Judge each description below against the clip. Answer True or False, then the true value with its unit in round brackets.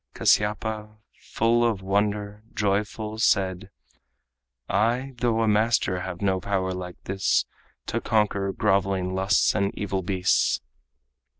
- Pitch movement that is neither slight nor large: False (2.2 semitones)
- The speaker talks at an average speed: False (115 wpm)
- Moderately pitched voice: False (100 Hz)